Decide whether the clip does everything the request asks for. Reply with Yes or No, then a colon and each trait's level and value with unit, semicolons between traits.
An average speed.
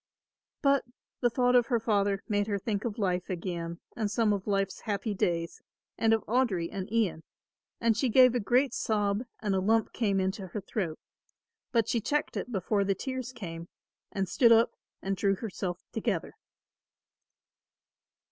Yes: average, 165 wpm